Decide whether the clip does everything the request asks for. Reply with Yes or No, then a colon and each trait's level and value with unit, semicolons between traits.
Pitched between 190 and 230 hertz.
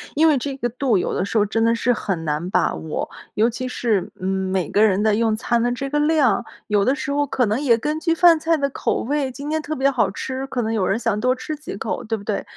No: high, 240 Hz